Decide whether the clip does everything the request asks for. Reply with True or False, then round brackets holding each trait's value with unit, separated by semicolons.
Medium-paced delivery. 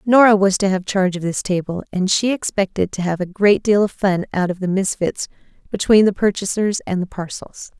False (215 wpm)